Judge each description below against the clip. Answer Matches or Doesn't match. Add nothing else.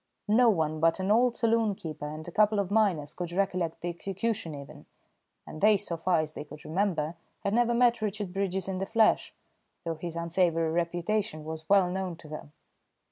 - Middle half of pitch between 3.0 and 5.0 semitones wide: Matches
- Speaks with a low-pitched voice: Doesn't match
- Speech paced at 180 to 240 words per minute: Matches